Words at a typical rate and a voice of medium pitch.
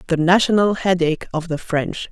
Yes: average, 170 wpm; medium, 175 Hz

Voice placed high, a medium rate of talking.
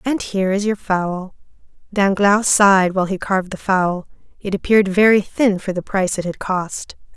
Yes: high, 195 Hz; average, 185 wpm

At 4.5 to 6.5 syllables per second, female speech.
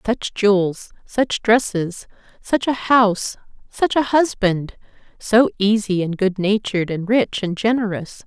No: 4.1 syllables/s; female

